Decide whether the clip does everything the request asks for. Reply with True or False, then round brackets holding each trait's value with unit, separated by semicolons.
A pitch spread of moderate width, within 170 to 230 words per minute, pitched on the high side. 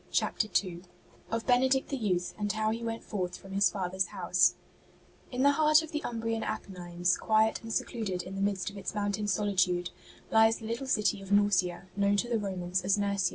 True (3.2 semitones; 200 wpm; 205 Hz)